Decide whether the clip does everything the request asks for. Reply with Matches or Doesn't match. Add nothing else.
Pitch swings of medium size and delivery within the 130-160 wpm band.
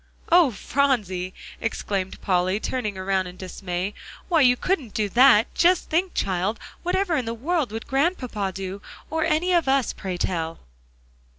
Doesn't match